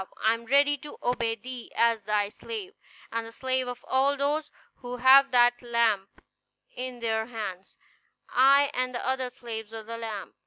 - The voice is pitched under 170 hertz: No, high, 245 Hz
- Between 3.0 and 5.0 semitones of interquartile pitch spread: No, narrow, 2.6 semitones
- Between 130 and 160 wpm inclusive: No, average, 170 wpm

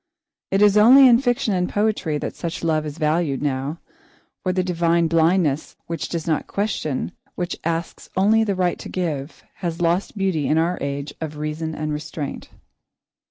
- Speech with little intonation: No, average, 3.6 semitones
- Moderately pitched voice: Yes, medium, 170 Hz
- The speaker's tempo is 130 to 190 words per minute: Yes, average, 170 wpm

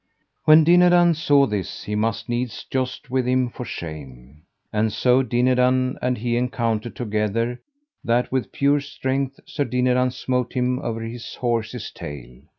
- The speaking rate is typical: Yes, average, 150 wpm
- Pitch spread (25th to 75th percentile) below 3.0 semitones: Yes, narrow, 2.4 semitones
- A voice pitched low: Yes, low, 125 Hz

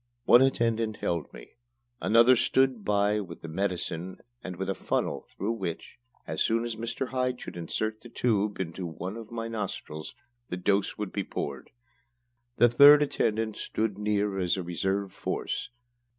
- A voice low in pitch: Yes, low, 105 Hz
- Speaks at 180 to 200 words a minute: No, average, 165 wpm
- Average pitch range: Yes, average, 3.7 semitones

